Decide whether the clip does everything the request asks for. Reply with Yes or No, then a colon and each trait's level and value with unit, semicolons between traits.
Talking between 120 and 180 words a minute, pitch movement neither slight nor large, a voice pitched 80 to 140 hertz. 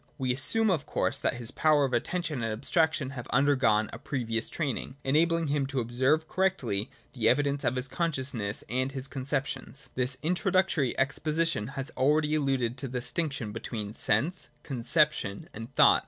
Yes: average, 165 wpm; average, 4.1 semitones; low, 135 Hz